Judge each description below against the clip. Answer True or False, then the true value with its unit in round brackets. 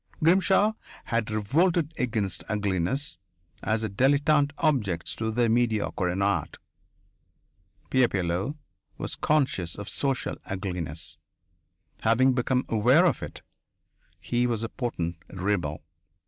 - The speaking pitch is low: True (115 Hz)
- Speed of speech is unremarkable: False (115 wpm)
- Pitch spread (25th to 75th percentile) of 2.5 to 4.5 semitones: False (5.6 semitones)